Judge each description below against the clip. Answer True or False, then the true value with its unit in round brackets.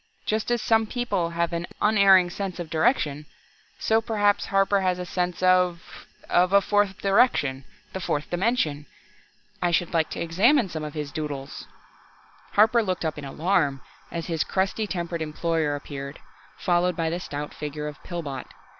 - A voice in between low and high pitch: True (175 Hz)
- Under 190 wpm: True (165 wpm)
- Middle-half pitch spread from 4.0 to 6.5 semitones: True (4.4 semitones)